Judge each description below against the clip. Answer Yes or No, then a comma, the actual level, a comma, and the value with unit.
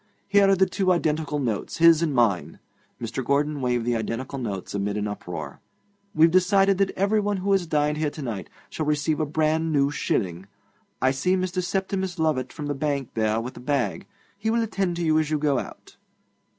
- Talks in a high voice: No, medium, 150 Hz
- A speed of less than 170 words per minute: No, average, 200 wpm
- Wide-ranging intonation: Yes, wide, 6.8 semitones